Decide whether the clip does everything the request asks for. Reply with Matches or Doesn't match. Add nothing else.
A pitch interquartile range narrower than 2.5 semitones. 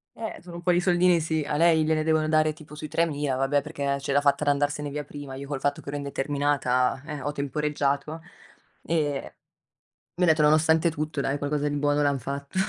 Matches